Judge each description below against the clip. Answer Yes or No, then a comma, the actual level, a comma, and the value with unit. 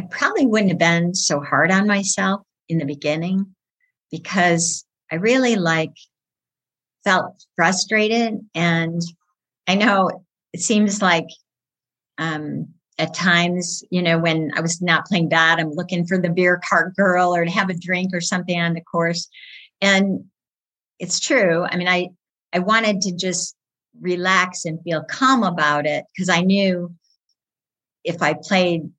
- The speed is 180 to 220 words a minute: No, average, 155 wpm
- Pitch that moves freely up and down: No, narrow, 2.5 semitones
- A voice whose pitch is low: No, medium, 180 Hz